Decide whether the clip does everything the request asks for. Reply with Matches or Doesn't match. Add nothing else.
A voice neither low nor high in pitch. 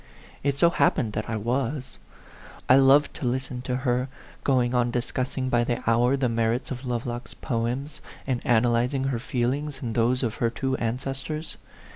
Doesn't match